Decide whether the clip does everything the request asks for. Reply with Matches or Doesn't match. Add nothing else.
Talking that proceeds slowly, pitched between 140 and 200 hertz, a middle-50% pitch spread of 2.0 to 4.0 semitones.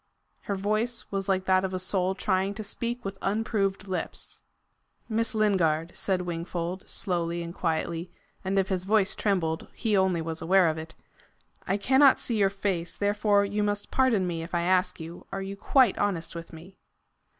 Doesn't match